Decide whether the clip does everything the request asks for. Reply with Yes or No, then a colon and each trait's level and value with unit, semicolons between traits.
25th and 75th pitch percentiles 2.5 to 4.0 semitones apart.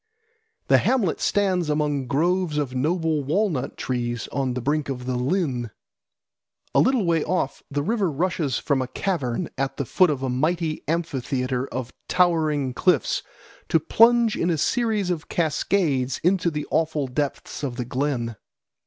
No: average, 5.3 semitones